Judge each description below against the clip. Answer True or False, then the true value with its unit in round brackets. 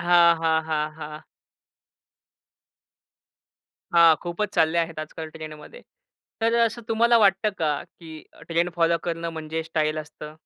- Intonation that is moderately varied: False (2.0 semitones)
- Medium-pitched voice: True (165 Hz)